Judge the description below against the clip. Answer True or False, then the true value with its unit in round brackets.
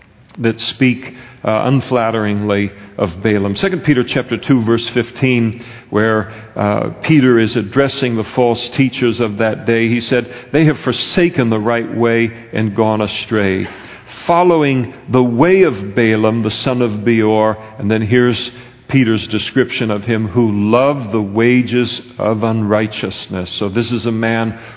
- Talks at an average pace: True (150 wpm)